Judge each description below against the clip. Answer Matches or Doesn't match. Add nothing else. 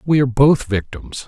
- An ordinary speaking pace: Matches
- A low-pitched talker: Matches